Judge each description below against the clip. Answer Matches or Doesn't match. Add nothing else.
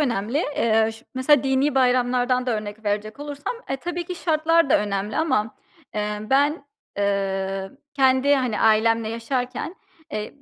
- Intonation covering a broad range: Doesn't match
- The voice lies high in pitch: Matches